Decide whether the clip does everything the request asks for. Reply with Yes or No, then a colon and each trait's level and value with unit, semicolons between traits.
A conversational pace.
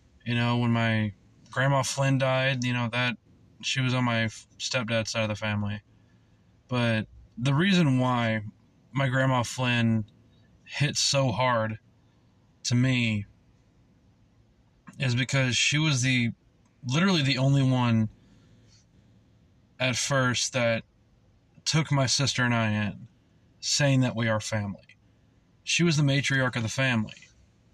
No: slow, 130 wpm